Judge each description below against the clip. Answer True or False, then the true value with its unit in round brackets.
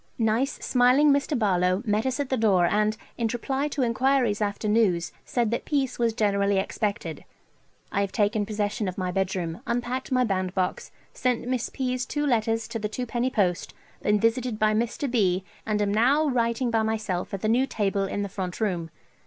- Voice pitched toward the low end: False (220 Hz)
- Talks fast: False (185 wpm)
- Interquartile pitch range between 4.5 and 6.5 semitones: False (3.8 semitones)